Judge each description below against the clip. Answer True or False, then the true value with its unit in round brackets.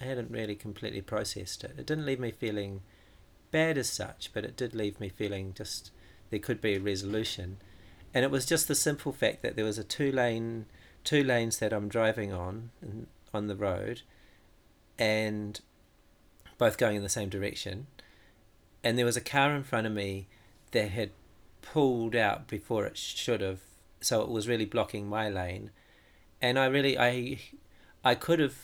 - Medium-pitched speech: False (105 Hz)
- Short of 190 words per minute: True (180 wpm)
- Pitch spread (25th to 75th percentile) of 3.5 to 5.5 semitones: True (3.8 semitones)